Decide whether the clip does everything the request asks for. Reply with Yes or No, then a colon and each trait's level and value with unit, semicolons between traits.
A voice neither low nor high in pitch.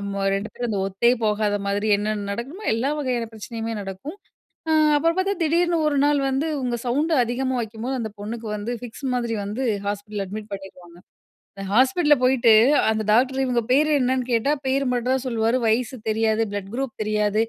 No: high, 235 Hz